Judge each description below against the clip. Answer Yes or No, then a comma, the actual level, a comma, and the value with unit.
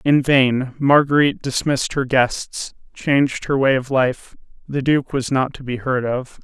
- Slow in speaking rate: No, average, 175 wpm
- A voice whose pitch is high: No, low, 135 Hz